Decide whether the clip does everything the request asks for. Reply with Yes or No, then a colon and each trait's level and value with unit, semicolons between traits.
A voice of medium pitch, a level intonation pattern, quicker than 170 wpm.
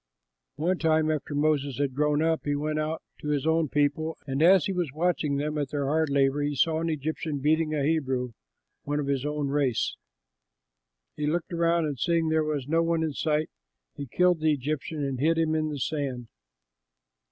Yes: medium, 150 Hz; narrow, 2.0 semitones; average, 200 wpm